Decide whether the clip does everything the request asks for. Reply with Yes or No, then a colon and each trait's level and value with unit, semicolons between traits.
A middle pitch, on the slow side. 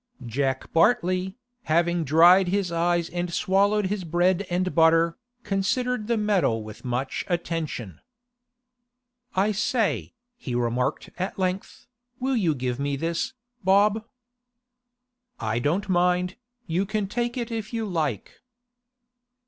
Yes: medium, 180 Hz; slow, 125 wpm